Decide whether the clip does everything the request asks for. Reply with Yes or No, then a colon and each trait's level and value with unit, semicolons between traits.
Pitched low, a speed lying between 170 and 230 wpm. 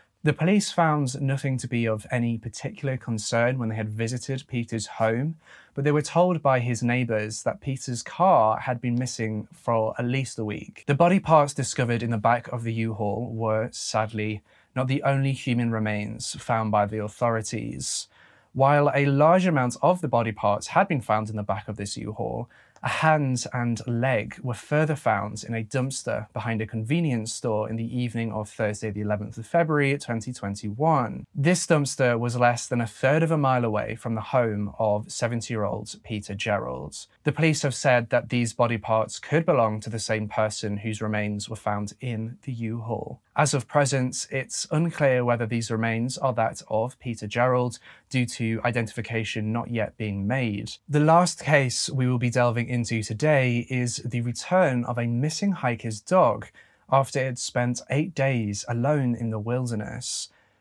Yes: low, 120 Hz; average, 185 wpm